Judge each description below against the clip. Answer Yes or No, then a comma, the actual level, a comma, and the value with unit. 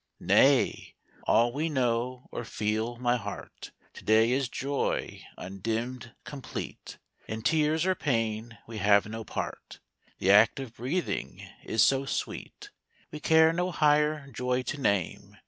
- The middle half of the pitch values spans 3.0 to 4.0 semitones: No, average, 4.7 semitones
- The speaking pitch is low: Yes, low, 125 Hz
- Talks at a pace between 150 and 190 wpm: No, average, 140 wpm